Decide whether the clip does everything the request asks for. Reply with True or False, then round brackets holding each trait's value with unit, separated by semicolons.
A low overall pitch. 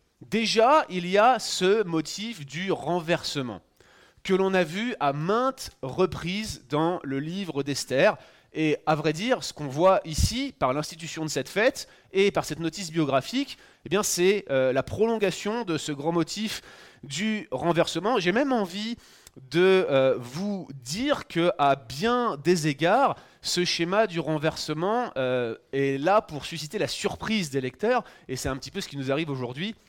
False (170 Hz)